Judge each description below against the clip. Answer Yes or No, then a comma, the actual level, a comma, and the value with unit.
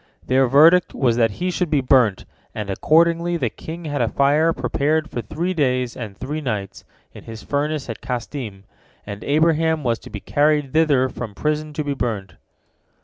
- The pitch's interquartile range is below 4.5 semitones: No, average, 4.8 semitones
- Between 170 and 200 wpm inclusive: Yes, average, 180 wpm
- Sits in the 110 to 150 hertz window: Yes, medium, 140 Hz